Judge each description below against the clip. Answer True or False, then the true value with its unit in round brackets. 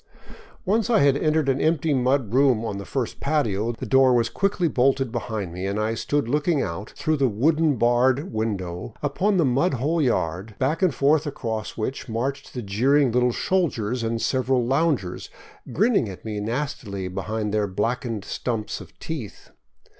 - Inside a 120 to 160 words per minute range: False (175 wpm)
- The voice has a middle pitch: False (125 Hz)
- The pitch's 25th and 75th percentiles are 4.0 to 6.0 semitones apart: True (4.9 semitones)